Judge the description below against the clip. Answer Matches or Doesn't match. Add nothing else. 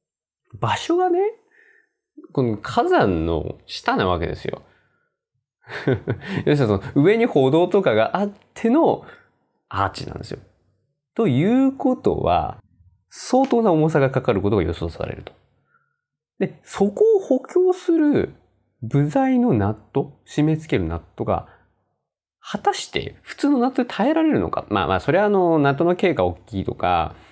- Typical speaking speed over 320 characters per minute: Doesn't match